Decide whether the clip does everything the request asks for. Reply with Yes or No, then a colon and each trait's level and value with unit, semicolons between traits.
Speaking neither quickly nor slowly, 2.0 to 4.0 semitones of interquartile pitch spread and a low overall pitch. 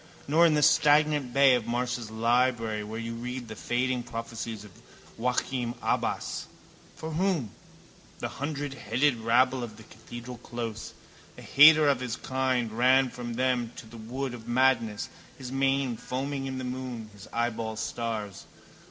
Yes: average, 150 wpm; narrow, 2.5 semitones; low, 125 Hz